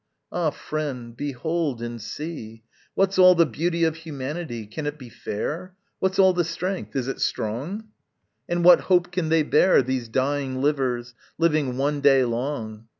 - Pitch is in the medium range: Yes, medium, 145 Hz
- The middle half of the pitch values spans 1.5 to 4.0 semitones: No, average, 5.2 semitones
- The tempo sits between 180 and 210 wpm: No, average, 160 wpm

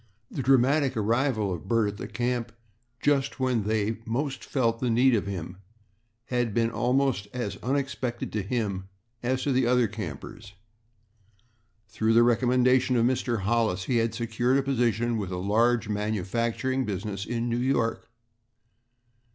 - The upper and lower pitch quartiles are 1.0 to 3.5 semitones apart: Yes, average, 2.9 semitones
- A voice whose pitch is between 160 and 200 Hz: No, low, 115 Hz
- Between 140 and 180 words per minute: Yes, average, 150 wpm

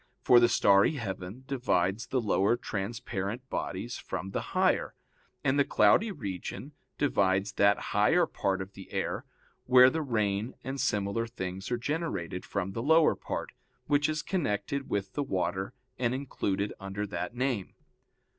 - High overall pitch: No, low, 105 Hz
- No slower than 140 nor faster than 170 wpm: Yes, average, 150 wpm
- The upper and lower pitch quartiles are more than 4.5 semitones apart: Yes, average, 5.3 semitones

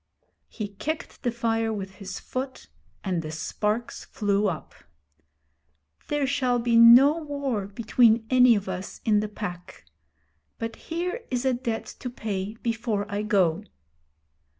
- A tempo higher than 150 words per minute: No, average, 140 wpm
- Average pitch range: Yes, average, 3.6 semitones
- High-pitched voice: Yes, high, 225 Hz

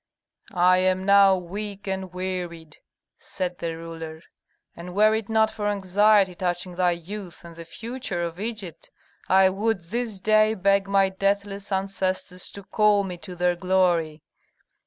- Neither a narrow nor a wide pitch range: No, narrow, 2.3 semitones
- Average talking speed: Yes, average, 150 wpm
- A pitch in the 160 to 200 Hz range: Yes, high, 190 Hz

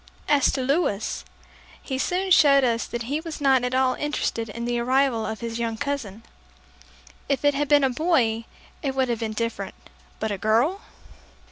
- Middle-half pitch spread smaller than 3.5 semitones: No, average, 3.8 semitones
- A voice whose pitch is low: No, very high, 255 Hz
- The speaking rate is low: No, average, 180 wpm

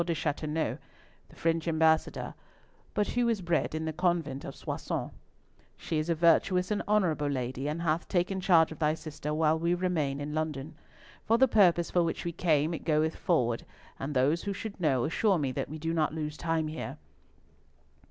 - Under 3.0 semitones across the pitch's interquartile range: Yes, narrow, 2.4 semitones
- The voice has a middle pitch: Yes, medium, 160 Hz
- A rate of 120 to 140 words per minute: No, average, 190 wpm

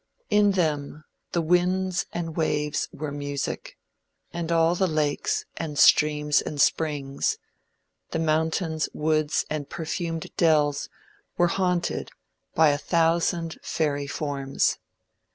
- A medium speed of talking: No, slow, 115 wpm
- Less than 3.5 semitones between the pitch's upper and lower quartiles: Yes, narrow, 2.4 semitones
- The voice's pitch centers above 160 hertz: No, medium, 155 Hz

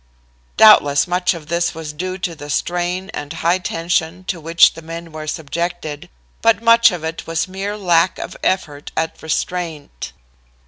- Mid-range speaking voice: Yes, medium, 170 Hz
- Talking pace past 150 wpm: Yes, average, 170 wpm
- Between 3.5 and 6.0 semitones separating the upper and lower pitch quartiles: No, narrow, 2.4 semitones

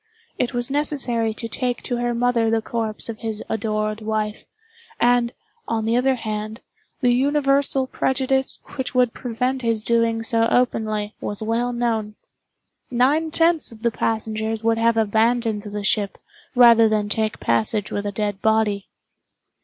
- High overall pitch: Yes, high, 230 Hz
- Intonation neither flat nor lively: No, narrow, 2.2 semitones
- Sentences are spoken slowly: No, average, 155 wpm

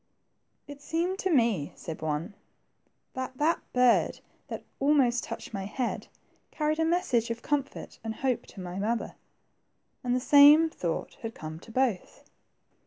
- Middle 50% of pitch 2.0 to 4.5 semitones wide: No, average, 5.0 semitones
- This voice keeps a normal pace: Yes, average, 155 wpm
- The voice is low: No, very high, 250 Hz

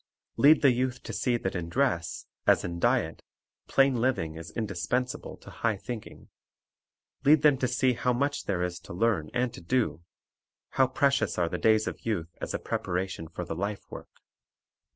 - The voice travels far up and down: Yes, wide, 6.6 semitones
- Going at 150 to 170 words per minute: No, average, 180 wpm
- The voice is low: Yes, low, 115 Hz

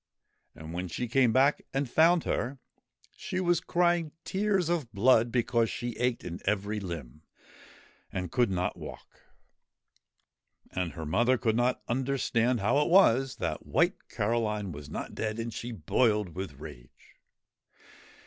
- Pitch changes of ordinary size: No, wide, 5.9 semitones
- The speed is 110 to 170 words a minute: Yes, average, 145 wpm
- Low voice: Yes, low, 115 Hz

